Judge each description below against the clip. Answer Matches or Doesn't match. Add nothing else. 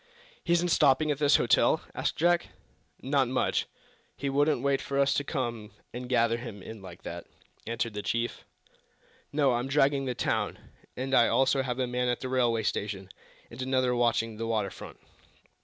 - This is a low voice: Matches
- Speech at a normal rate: Matches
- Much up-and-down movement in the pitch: Doesn't match